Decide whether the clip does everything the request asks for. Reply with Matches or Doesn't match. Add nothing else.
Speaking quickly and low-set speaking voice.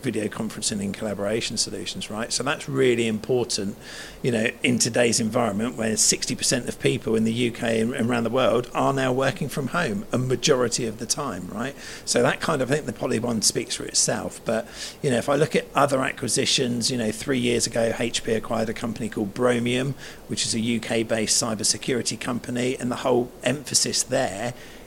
Doesn't match